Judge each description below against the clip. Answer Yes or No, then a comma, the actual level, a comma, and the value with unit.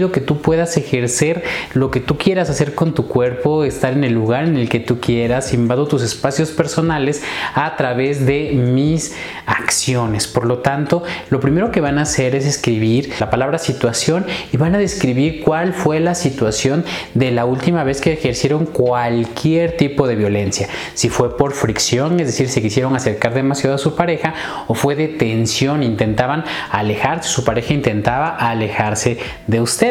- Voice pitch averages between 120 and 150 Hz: Yes, low, 135 Hz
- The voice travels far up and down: No, average, 4.4 semitones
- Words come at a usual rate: Yes, average, 175 wpm